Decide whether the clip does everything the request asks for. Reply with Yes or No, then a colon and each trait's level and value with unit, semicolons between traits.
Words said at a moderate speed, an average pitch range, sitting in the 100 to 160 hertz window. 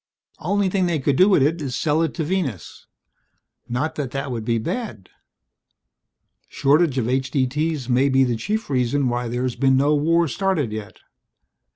Yes: average, 170 wpm; average, 4.7 semitones; medium, 140 Hz